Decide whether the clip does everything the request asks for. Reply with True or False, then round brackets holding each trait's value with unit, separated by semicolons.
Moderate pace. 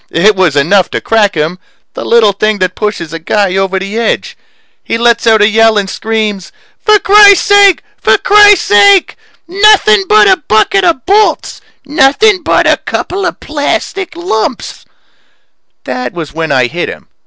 True (165 wpm)